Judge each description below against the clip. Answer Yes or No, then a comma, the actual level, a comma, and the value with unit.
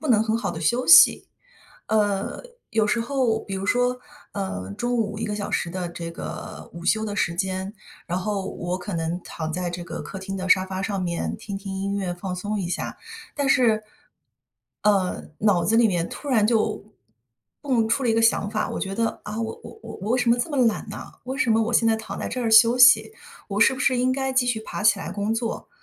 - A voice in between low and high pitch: No, high, 210 Hz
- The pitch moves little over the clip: No, average, 3.6 semitones